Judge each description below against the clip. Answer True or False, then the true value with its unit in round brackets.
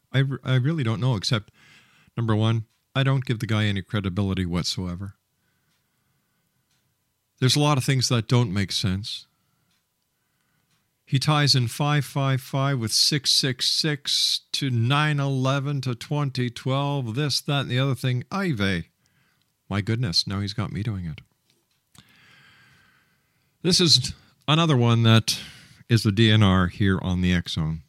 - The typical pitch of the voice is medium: False (125 Hz)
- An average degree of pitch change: True (4.7 semitones)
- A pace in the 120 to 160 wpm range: True (140 wpm)